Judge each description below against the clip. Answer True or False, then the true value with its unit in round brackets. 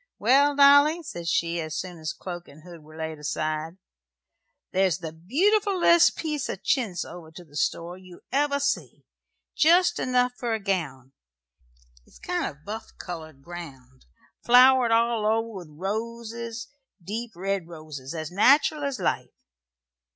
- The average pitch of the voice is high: True (195 Hz)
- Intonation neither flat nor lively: False (7.8 semitones)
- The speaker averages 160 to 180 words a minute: False (145 wpm)